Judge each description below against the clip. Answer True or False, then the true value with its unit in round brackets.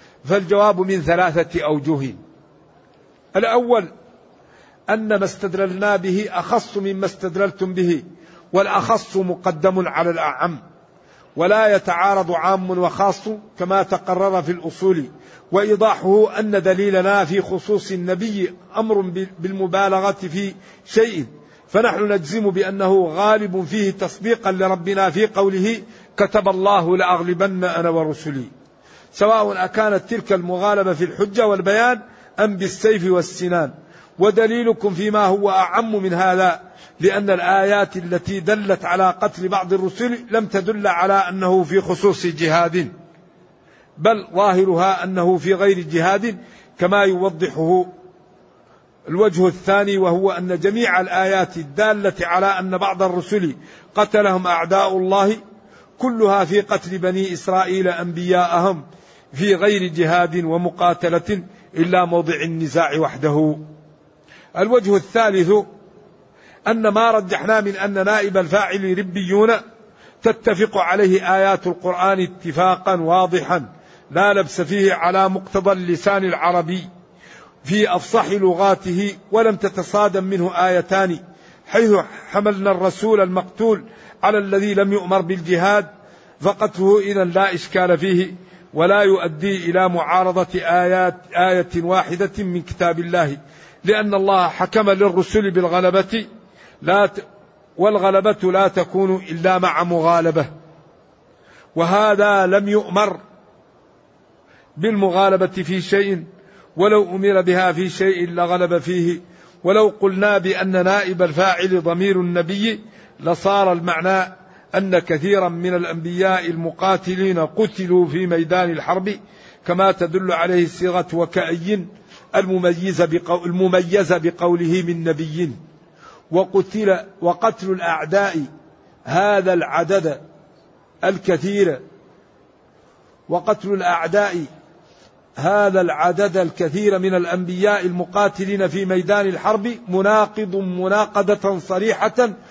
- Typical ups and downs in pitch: False (2.1 semitones)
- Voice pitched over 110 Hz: True (190 Hz)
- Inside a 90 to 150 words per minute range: True (100 wpm)